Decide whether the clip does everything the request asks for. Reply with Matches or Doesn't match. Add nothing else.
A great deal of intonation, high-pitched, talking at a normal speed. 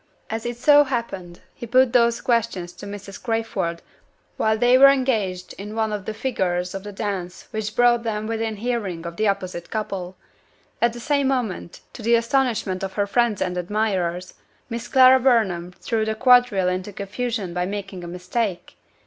Doesn't match